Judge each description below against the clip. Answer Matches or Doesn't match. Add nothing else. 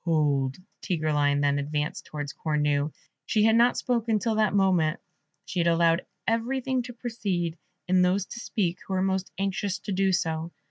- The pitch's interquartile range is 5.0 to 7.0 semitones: Matches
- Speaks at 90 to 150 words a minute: Doesn't match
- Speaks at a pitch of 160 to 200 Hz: Matches